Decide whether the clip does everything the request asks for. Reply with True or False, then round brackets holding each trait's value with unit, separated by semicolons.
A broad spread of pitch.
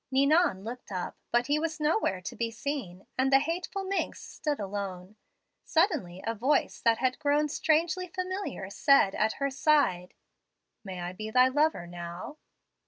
True (7.8 semitones)